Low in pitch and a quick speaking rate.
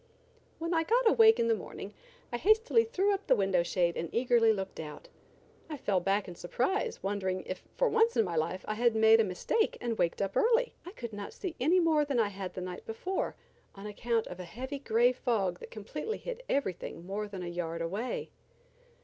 No: high, 225 Hz; fast, 210 wpm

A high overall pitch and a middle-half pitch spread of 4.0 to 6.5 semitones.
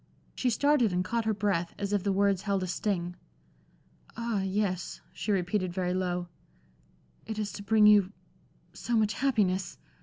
No: high, 200 Hz; average, 2.7 semitones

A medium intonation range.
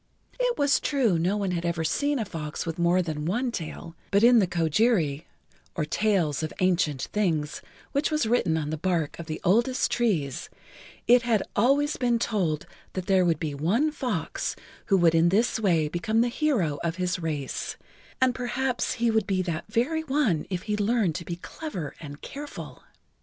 No: wide, 6.6 semitones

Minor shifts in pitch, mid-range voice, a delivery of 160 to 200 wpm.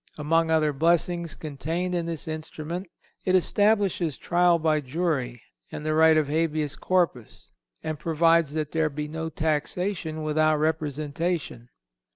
No: narrow, 1.9 semitones; medium, 160 Hz; average, 140 wpm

